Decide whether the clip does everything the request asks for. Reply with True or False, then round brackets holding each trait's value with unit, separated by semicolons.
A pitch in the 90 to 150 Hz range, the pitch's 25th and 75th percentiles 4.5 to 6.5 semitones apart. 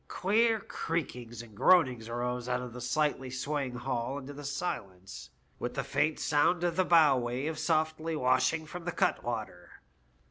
True (140 Hz; 4.8 semitones)